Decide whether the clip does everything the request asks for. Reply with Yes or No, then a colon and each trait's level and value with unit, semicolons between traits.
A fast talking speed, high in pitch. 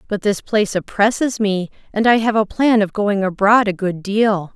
Yes: fast, 210 wpm; high, 205 Hz